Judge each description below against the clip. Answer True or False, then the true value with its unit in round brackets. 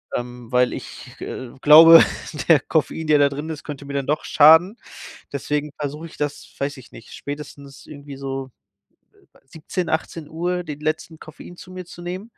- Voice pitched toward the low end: False (150 Hz)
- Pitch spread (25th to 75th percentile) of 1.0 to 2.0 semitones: False (2.7 semitones)